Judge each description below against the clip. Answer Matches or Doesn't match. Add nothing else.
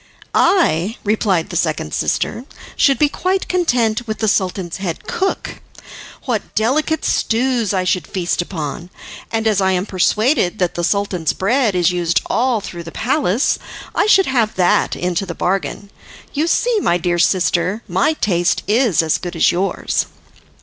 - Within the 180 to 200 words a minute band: Doesn't match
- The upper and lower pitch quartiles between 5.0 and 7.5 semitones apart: Matches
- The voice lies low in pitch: Doesn't match